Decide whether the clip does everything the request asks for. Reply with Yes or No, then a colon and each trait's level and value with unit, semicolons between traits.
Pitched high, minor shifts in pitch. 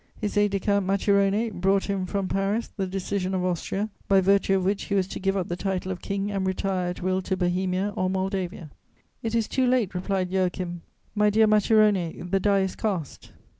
Yes: high, 195 Hz; narrow, 1.5 semitones